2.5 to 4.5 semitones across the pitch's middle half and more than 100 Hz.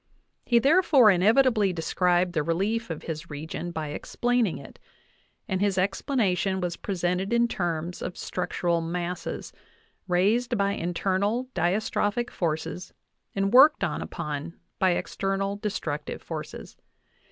Yes: average, 3.9 semitones; high, 190 Hz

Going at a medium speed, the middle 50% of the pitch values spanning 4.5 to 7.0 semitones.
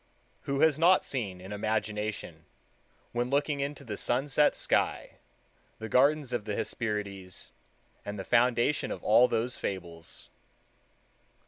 No: slow, 125 wpm; average, 5.1 semitones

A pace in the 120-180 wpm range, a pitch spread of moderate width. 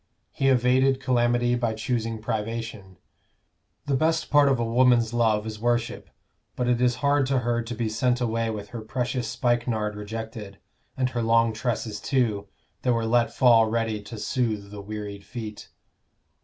No: average, 165 wpm; narrow, 2.2 semitones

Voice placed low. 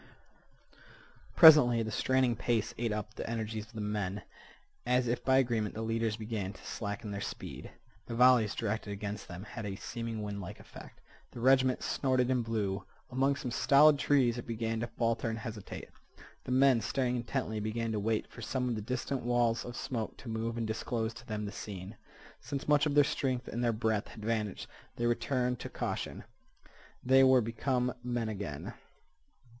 Yes: low, 115 Hz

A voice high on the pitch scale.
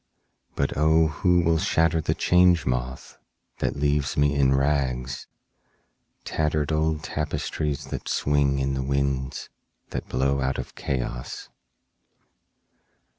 No: very low, 70 Hz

